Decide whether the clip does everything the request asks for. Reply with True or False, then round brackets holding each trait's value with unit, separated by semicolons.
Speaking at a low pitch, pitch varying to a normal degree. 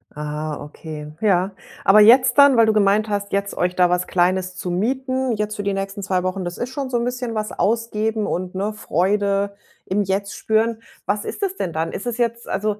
False (205 Hz; 3.5 semitones)